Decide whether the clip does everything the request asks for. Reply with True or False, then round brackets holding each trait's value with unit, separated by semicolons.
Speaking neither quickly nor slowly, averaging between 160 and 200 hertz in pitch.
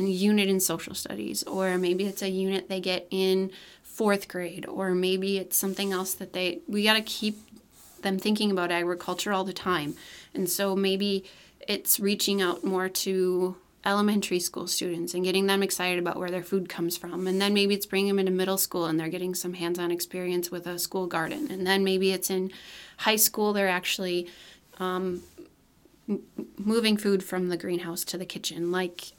True (190 wpm; 185 Hz)